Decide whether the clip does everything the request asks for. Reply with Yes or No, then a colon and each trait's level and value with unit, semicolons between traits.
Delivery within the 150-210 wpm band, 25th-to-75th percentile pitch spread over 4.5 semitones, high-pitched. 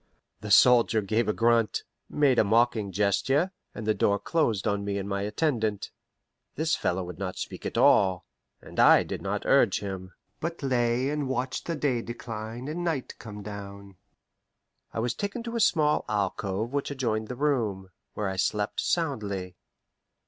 No: average, 170 wpm; average, 5.2 semitones; low, 110 Hz